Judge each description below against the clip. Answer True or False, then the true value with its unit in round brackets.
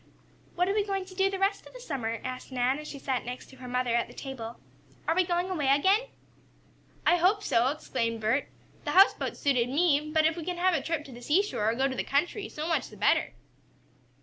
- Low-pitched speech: False (300 Hz)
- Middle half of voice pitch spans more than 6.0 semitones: True (6.4 semitones)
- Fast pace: True (235 wpm)